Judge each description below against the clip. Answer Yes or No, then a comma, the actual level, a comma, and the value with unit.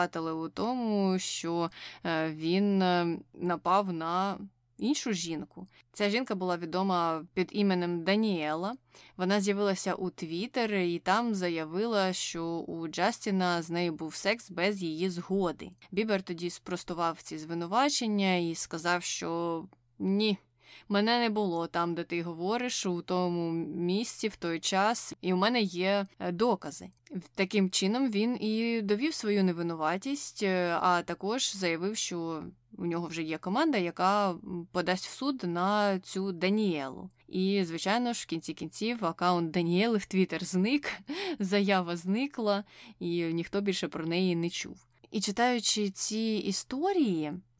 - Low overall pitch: No, medium, 185 Hz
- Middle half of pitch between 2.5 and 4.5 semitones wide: Yes, average, 3.3 semitones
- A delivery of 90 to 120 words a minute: No, average, 135 wpm